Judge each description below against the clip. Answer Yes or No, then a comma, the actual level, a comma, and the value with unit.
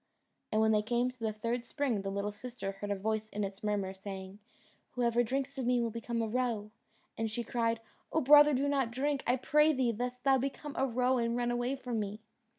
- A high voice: Yes, high, 235 Hz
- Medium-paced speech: No, fast, 225 wpm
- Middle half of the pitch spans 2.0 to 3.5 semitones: Yes, average, 3.2 semitones